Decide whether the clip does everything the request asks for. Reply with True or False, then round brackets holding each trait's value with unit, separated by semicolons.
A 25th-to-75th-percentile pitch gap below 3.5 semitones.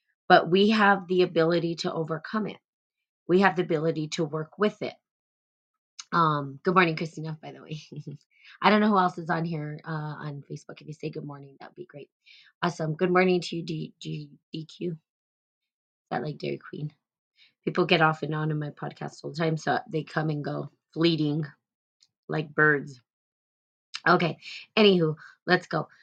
True (3.0 semitones)